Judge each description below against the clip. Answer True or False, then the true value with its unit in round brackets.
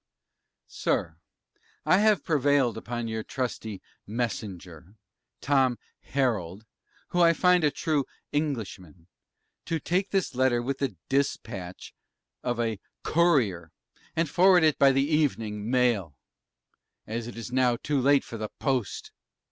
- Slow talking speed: True (130 wpm)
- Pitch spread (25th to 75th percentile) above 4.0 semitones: True (5.1 semitones)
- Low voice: True (125 Hz)